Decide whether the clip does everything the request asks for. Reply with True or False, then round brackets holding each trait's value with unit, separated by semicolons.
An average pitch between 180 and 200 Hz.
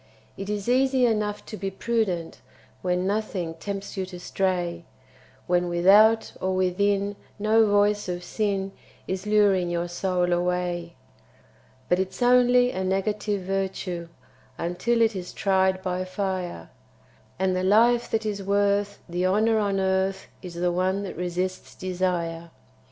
True (190 Hz)